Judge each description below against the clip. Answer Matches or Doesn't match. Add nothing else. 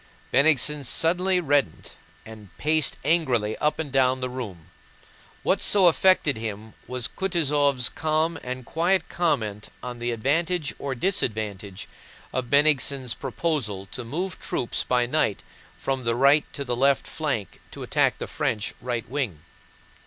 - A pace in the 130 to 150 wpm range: Matches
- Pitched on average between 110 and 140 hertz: Matches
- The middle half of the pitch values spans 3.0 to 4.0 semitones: Doesn't match